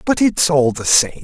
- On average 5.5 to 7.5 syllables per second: No, 4.5 syllables/s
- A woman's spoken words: No, male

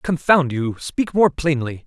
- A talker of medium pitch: Yes, medium, 150 Hz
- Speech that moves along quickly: No, average, 160 wpm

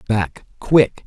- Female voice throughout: No, male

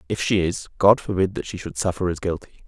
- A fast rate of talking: Yes, fast, 245 wpm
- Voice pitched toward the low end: Yes, very low, 95 Hz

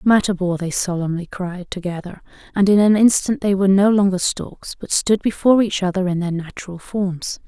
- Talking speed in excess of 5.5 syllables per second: No, 5.3 syllables/s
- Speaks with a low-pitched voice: No, high, 190 Hz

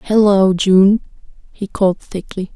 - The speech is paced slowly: Yes, slow, 115 wpm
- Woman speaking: Yes, female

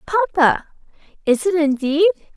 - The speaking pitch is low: No, very high, 335 Hz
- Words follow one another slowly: Yes, slow, 100 wpm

